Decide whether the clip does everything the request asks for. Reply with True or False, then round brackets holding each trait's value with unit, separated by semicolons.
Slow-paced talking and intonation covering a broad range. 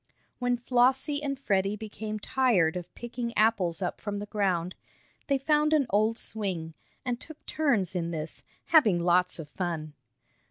False (155 wpm; 5.8 semitones)